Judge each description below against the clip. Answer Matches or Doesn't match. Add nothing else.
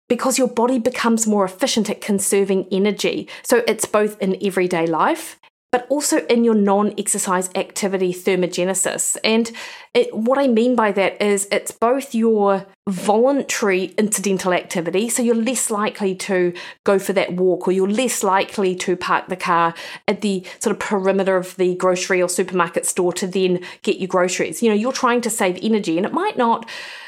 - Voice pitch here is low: Doesn't match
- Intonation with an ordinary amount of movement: Matches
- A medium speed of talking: Matches